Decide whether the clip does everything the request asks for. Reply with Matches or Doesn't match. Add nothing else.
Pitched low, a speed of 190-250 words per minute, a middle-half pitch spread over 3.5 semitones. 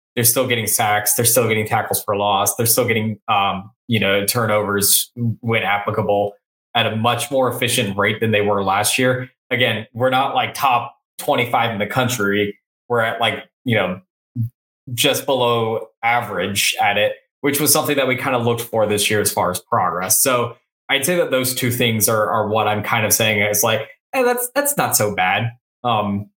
Doesn't match